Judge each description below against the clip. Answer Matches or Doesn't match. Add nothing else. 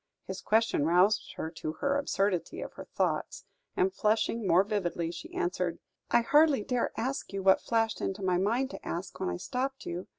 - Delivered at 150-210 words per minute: Matches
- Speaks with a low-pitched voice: Doesn't match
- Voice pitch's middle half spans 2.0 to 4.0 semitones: Doesn't match